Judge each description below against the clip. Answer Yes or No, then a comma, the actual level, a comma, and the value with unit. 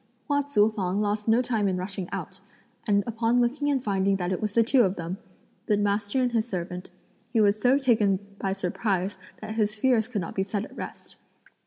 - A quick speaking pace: Yes, fast, 210 wpm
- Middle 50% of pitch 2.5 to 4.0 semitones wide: Yes, average, 3.2 semitones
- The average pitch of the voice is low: No, high, 210 Hz